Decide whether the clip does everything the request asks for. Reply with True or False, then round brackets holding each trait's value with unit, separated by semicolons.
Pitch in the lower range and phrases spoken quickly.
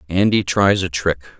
False (90 Hz; 170 wpm)